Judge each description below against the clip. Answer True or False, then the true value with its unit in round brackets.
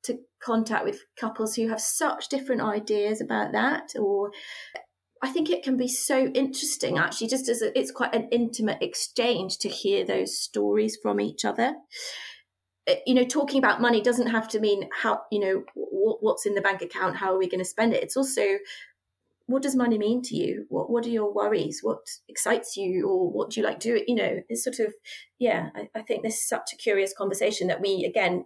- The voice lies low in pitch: False (235 Hz)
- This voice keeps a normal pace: False (215 wpm)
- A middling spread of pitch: True (4.7 semitones)